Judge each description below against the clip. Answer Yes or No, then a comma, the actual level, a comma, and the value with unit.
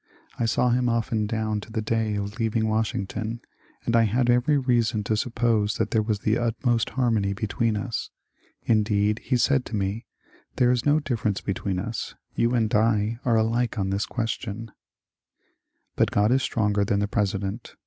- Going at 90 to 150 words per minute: No, average, 180 wpm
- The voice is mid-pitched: No, low, 110 Hz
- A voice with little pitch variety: Yes, narrow, 2.2 semitones